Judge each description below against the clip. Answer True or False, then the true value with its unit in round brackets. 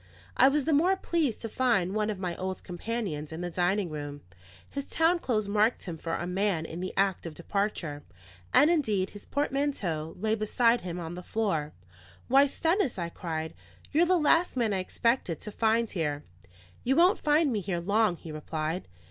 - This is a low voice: False (205 Hz)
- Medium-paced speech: True (190 wpm)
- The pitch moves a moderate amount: False (7.1 semitones)